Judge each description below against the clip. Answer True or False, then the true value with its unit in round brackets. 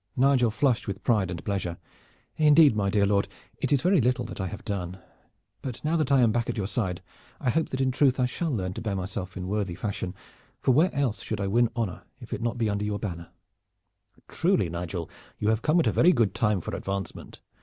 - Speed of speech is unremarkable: False (230 wpm)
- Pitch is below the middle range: True (110 Hz)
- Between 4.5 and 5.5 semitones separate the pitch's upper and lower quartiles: True (5.0 semitones)